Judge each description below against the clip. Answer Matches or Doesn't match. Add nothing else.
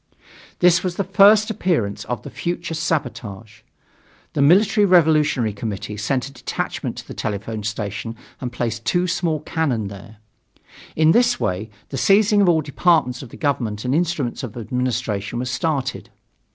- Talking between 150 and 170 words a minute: Matches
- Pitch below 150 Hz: Matches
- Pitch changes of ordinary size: Doesn't match